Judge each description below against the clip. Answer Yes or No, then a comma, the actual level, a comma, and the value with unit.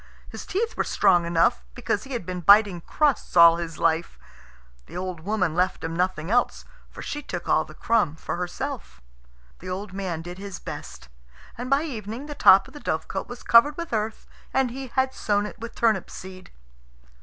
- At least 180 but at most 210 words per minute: Yes, average, 190 wpm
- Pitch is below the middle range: No, high, 200 Hz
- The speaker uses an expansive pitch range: Yes, wide, 5.7 semitones